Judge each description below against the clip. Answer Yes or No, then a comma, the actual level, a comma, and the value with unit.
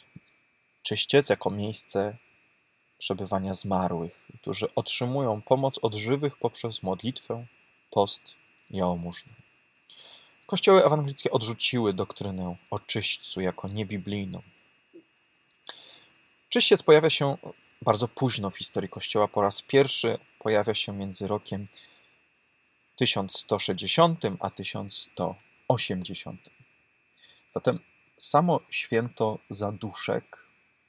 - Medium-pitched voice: No, low, 110 Hz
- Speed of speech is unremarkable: No, slow, 85 wpm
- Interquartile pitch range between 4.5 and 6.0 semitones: Yes, average, 5.0 semitones